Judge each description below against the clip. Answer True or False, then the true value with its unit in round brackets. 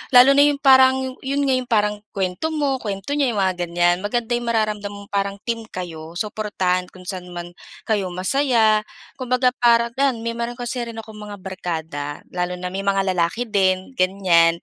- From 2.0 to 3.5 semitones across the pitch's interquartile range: False (4.8 semitones)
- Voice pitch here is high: True (210 Hz)